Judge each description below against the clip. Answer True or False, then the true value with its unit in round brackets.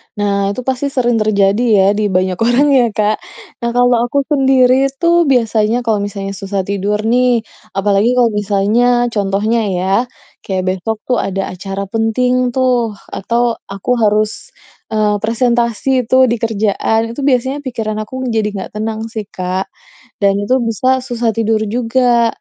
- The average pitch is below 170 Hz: False (225 Hz)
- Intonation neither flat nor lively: True (3.4 semitones)